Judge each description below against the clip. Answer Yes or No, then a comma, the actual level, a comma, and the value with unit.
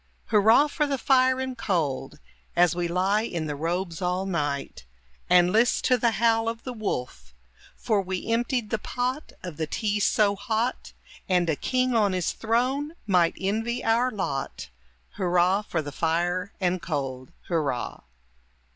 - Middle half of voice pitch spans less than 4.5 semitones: No, average, 5.1 semitones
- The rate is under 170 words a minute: Yes, average, 155 wpm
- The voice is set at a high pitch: Yes, high, 195 Hz